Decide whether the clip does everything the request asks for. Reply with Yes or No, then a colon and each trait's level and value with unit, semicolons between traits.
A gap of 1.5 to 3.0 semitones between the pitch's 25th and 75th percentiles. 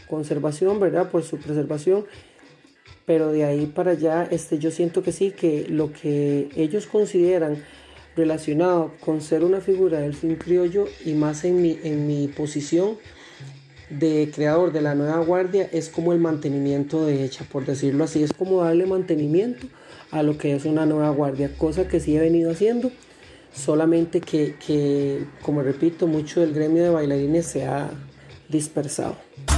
Yes: narrow, 2.6 semitones